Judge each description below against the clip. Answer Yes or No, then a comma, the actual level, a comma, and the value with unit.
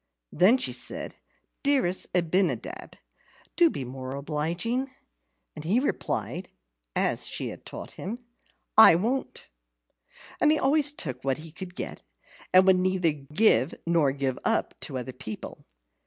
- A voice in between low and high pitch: Yes, medium, 175 Hz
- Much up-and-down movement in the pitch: Yes, wide, 8.2 semitones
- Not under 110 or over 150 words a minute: Yes, slow, 135 wpm